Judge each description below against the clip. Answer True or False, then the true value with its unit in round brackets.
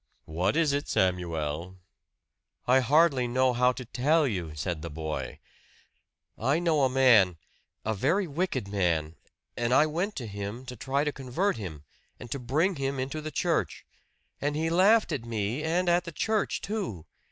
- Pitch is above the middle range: False (130 Hz)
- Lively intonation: True (7.6 semitones)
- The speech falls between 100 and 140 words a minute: False (170 wpm)